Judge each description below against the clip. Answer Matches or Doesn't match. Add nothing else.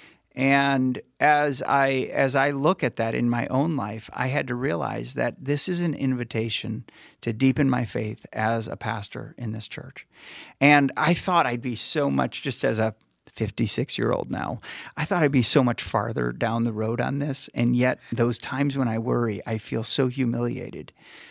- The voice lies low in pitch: Matches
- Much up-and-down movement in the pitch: Doesn't match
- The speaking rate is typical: Matches